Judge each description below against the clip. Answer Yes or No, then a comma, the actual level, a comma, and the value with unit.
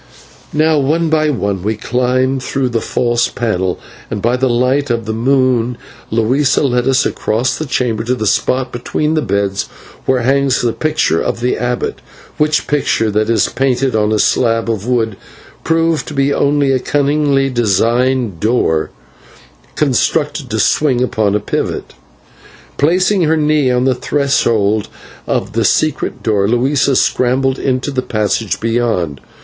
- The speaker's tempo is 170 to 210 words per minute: No, average, 155 wpm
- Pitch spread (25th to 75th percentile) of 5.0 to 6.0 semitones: No, average, 3.7 semitones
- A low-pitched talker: Yes, low, 125 Hz